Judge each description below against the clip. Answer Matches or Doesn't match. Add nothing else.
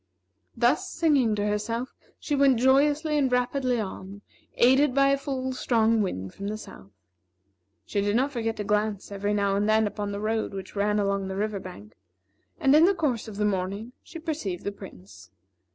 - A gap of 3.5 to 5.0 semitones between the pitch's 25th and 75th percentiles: Matches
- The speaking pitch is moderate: Doesn't match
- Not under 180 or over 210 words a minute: Matches